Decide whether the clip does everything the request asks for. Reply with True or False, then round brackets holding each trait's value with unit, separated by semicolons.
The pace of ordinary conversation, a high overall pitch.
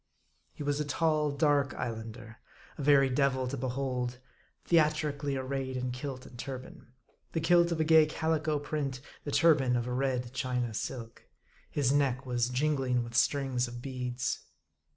False (160 wpm; 135 Hz)